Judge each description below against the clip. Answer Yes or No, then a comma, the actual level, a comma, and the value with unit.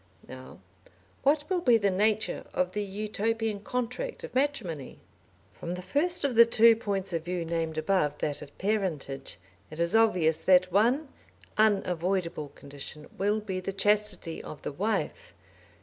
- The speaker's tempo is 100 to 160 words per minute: Yes, average, 150 wpm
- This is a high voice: Yes, high, 195 Hz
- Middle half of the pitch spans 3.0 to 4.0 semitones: No, average, 4.9 semitones